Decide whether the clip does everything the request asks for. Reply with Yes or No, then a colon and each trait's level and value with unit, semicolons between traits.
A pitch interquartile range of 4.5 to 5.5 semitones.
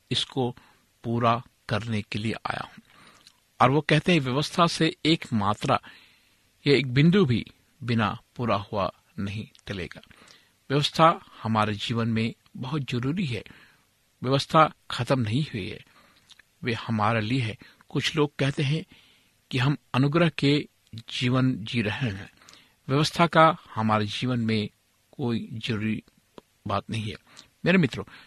Yes: average, 4.8 semitones